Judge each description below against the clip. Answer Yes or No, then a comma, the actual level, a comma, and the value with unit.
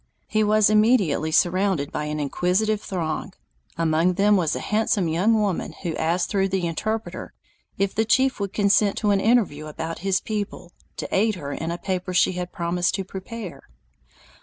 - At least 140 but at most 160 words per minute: No, average, 175 wpm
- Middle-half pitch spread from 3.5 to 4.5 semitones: Yes, average, 3.9 semitones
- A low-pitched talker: No, high, 190 Hz